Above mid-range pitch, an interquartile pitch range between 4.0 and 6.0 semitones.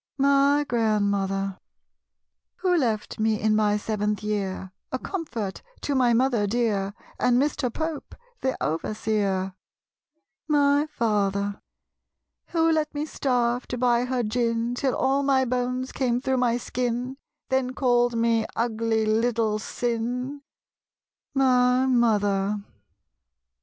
No: high, 240 Hz; average, 3.5 semitones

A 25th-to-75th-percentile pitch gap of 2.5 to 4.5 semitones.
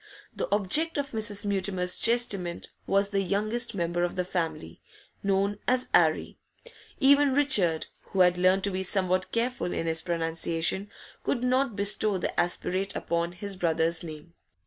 Yes: average, 3.4 semitones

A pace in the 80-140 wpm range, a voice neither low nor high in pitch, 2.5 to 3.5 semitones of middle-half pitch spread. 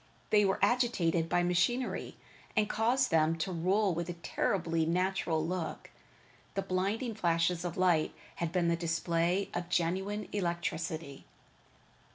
Yes: slow, 135 wpm; medium, 175 Hz; average, 2.8 semitones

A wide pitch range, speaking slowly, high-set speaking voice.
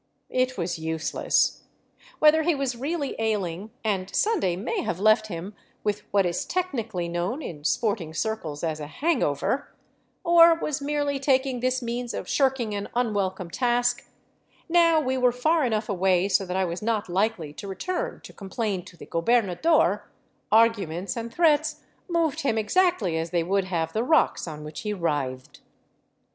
No: wide, 7.1 semitones; average, 175 wpm; high, 220 Hz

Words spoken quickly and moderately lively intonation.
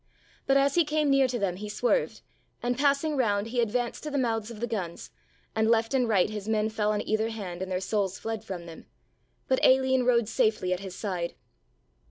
Yes: fast, 215 wpm; average, 4.0 semitones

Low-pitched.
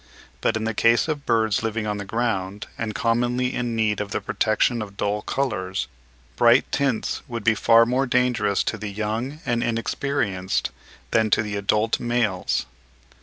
Yes: low, 115 Hz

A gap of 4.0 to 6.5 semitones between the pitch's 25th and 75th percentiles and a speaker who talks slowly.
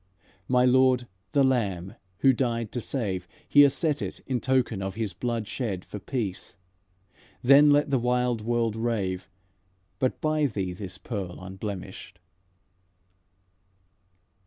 Yes: average, 5.1 semitones; slow, 130 wpm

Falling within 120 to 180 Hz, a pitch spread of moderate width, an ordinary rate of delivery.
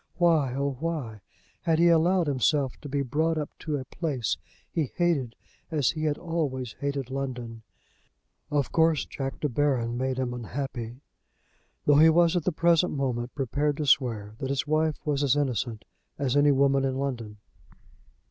Yes: medium, 140 Hz; average, 3.5 semitones; average, 165 wpm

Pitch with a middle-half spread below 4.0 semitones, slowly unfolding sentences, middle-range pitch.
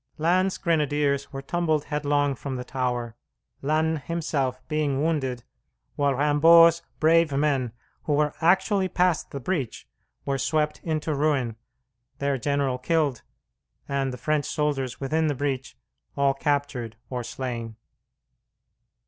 Yes: average, 2.9 semitones; slow, 125 wpm; medium, 145 Hz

